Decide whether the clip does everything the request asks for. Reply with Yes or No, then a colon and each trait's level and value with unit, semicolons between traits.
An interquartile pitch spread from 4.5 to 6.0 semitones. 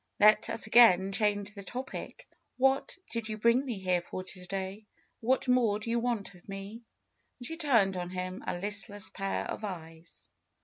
No: average, 3.6 semitones